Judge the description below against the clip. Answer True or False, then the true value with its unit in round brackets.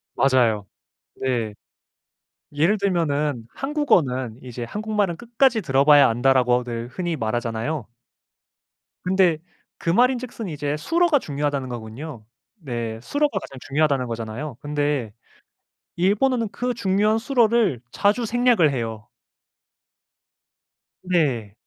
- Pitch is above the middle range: False (150 Hz)